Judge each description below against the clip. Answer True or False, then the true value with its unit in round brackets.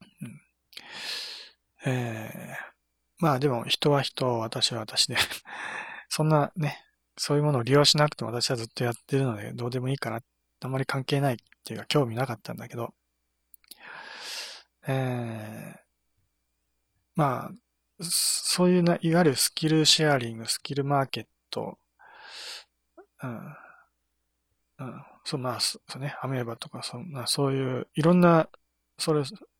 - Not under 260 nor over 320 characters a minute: True (270 characters per minute)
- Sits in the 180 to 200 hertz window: False (130 Hz)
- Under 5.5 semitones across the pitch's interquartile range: True (5.1 semitones)